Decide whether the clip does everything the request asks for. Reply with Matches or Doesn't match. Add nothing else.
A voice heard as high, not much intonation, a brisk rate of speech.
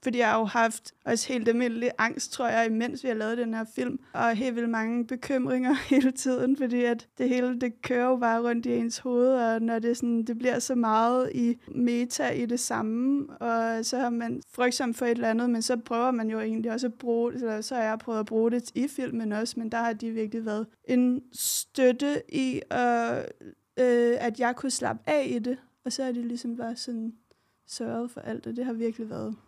Matches